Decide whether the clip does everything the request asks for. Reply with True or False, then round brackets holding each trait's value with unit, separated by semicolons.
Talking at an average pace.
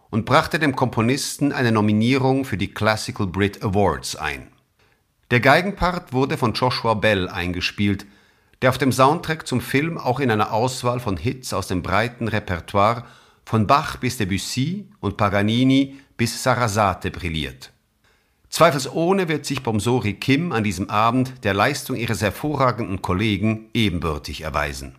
True (140 wpm)